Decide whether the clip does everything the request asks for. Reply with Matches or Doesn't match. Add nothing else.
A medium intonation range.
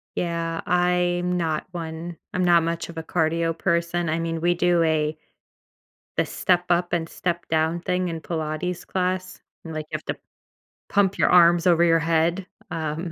Doesn't match